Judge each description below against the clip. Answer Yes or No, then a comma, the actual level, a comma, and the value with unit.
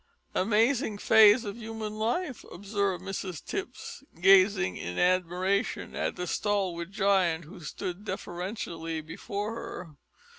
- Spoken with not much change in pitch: No, average, 3.6 semitones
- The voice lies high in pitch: Yes, high, 195 Hz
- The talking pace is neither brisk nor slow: No, slow, 115 wpm